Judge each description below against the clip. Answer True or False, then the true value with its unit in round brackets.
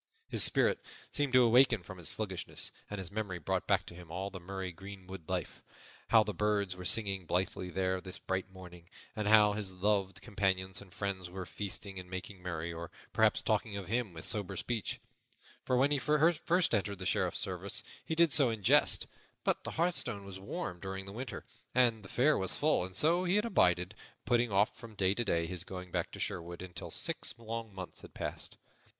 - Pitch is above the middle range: False (95 Hz)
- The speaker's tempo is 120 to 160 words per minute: False (205 wpm)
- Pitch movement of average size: True (3.6 semitones)